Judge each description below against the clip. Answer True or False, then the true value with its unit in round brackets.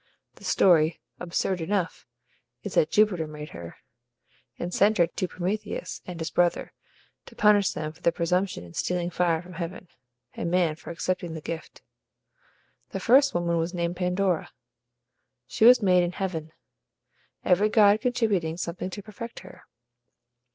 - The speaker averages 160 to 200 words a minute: False (150 wpm)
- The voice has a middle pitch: True (180 Hz)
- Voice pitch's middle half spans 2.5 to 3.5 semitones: True (2.9 semitones)